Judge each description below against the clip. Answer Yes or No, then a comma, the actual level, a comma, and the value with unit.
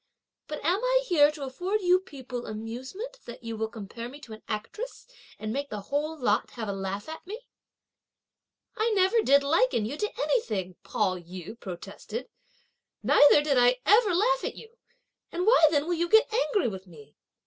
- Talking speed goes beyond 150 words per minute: Yes, average, 180 wpm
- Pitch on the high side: Yes, very high, 285 Hz